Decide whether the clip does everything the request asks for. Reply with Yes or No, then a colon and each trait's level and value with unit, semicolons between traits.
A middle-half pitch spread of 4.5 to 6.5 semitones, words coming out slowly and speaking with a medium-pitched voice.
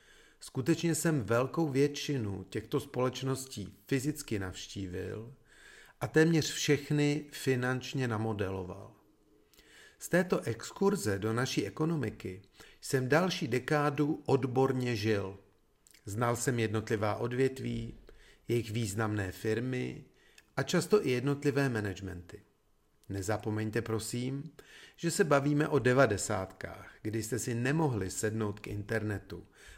No: average, 5.1 semitones; slow, 100 wpm; low, 125 Hz